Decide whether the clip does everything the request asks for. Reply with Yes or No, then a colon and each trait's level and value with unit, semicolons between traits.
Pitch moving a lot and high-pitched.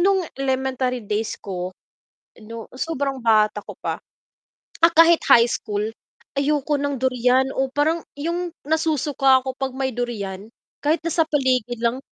No: average, 4.2 semitones; very high, 265 Hz